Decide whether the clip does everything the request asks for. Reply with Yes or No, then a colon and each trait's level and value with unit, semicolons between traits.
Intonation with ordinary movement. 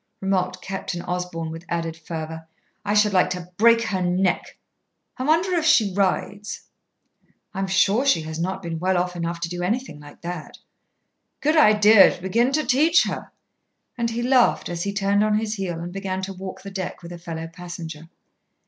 Yes: average, 3.6 semitones